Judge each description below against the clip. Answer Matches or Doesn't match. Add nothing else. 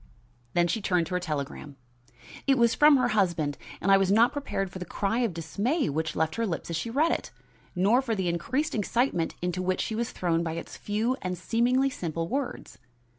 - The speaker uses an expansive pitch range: Matches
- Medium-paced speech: Doesn't match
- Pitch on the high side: Matches